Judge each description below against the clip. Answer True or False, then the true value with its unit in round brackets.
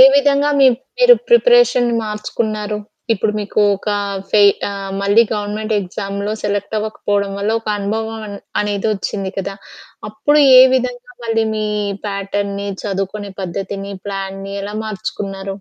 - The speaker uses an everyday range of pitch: False (1.9 semitones)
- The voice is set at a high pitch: True (205 Hz)